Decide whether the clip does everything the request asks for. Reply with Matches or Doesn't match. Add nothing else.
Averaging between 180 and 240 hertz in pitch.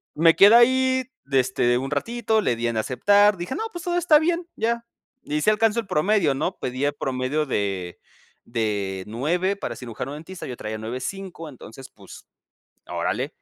Doesn't match